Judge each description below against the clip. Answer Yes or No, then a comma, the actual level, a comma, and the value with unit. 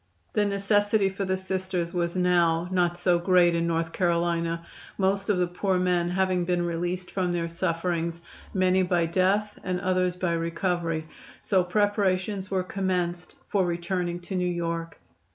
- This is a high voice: No, medium, 180 Hz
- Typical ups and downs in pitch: No, narrow, 1.7 semitones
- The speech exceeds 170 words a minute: No, average, 155 wpm